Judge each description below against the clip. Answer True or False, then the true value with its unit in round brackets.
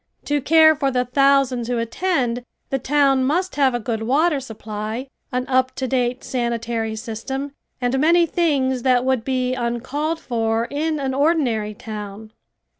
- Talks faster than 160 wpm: False (155 wpm)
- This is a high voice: True (255 Hz)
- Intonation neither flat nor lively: True (3.3 semitones)